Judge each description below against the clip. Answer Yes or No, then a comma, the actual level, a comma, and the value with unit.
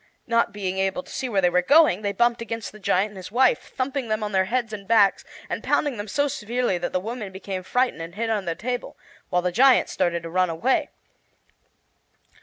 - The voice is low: No, high, 210 Hz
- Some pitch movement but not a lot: Yes, average, 4.5 semitones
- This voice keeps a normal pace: No, fast, 220 wpm